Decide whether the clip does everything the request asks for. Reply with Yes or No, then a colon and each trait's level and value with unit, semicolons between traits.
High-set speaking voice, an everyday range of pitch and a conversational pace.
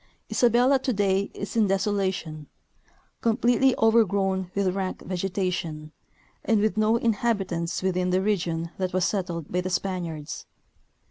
No: high, 195 Hz; average, 3.2 semitones; slow, 130 wpm